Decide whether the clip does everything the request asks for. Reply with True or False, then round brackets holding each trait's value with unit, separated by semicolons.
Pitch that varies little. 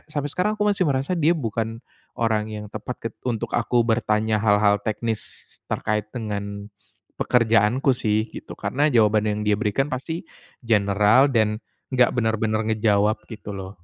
False (3.1 semitones)